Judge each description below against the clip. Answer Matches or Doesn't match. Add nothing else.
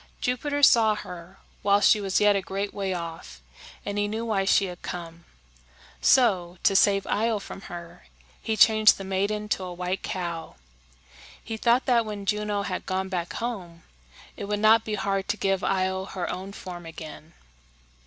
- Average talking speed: Matches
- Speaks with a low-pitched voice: Doesn't match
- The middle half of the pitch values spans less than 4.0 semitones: Matches